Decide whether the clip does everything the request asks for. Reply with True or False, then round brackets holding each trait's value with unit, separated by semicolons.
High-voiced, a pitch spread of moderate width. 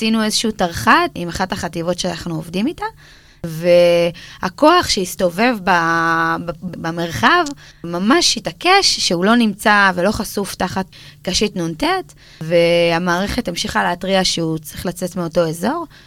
False (180 Hz; 4.5 semitones)